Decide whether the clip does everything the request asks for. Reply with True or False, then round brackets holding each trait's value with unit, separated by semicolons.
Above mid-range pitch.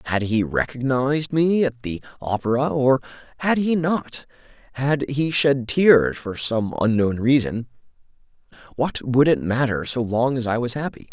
False (130 Hz)